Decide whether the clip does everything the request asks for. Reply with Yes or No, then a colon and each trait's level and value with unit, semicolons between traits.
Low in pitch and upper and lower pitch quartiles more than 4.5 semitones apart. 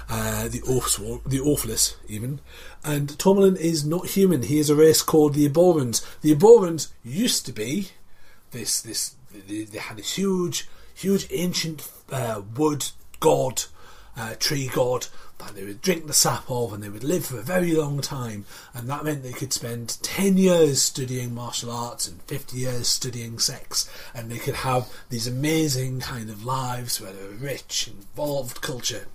Yes: low, 130 Hz; average, 4.9 semitones